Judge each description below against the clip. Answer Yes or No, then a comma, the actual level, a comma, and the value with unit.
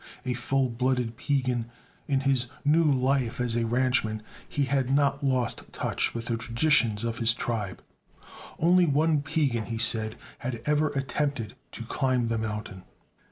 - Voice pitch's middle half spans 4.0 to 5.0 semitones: No, average, 3.3 semitones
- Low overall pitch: Yes, low, 125 Hz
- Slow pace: No, average, 155 wpm